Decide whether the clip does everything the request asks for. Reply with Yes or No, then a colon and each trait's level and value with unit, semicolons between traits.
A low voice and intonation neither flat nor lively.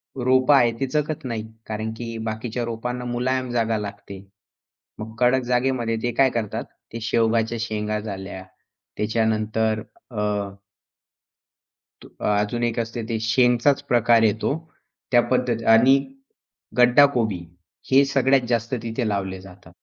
No: low, 115 Hz; narrow, 2.2 semitones